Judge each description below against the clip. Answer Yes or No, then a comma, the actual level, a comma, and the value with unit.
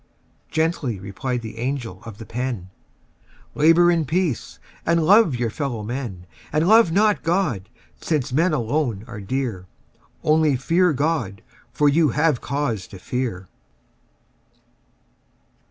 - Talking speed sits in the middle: No, slow, 125 wpm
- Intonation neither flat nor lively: No, wide, 6.3 semitones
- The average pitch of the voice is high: No, low, 135 Hz